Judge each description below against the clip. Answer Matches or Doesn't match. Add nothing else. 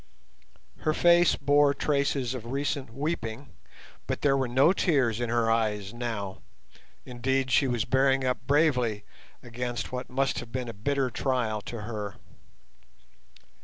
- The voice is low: Matches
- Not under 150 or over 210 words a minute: Doesn't match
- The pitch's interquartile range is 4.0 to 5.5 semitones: Doesn't match